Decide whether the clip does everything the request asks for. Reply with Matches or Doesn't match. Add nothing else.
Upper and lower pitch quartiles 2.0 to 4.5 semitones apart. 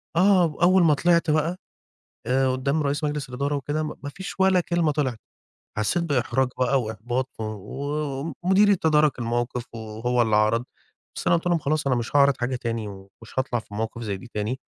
Doesn't match